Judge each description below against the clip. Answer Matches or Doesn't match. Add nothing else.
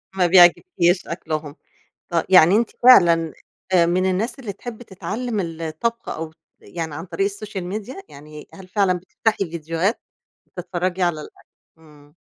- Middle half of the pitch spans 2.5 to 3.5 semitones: Doesn't match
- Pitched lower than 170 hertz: Doesn't match